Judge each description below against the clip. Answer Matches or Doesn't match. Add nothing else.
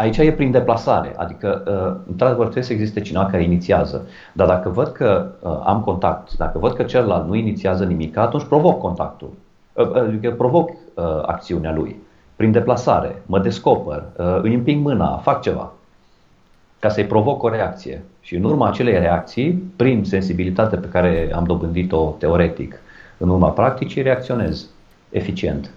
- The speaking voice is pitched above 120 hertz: Doesn't match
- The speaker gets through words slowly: Doesn't match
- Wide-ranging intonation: Matches